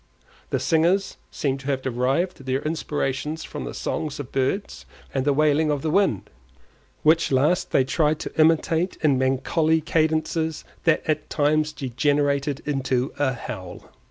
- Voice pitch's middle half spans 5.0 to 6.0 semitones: No, average, 3.0 semitones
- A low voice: No, medium, 150 Hz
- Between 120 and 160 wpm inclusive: Yes, average, 150 wpm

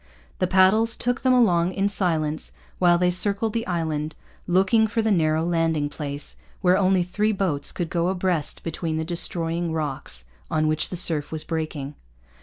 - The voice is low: No, medium, 175 Hz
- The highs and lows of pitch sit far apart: No, average, 3.4 semitones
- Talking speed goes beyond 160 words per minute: Yes, average, 170 wpm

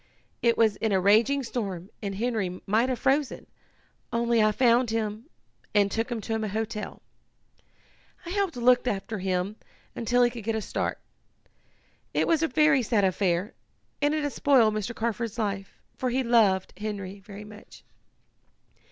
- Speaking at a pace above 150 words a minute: Yes, average, 160 wpm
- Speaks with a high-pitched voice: Yes, high, 225 Hz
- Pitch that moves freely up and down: No, average, 3.2 semitones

